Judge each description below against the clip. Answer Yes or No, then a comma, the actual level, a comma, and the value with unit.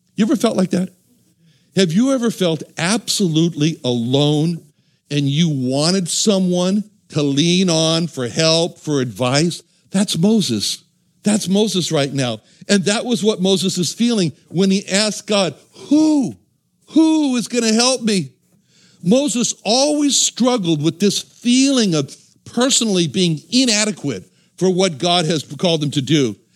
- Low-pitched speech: No, medium, 180 Hz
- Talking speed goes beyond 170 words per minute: No, average, 145 wpm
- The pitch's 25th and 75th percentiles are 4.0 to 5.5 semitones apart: Yes, average, 5.2 semitones